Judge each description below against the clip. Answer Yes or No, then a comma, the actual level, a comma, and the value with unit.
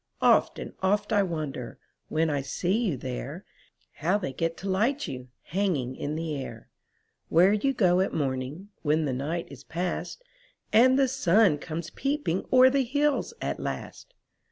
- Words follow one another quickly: No, average, 165 wpm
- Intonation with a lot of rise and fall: Yes, wide, 6.8 semitones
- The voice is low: No, medium, 175 Hz